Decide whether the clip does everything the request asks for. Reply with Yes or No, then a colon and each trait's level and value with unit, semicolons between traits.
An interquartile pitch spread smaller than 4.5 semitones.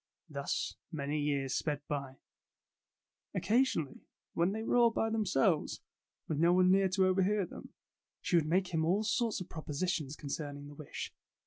No: average, 4.8 semitones